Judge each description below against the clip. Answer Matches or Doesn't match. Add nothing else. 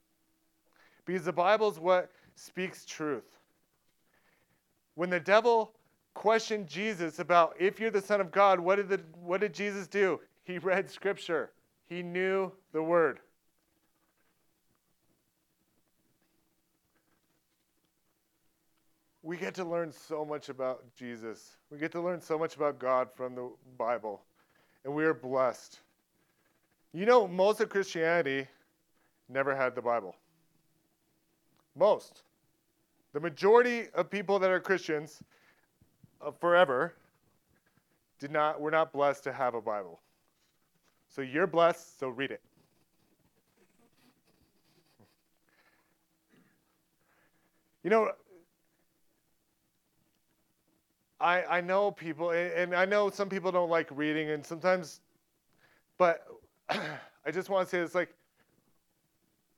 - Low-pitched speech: Doesn't match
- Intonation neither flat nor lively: Matches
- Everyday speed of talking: Doesn't match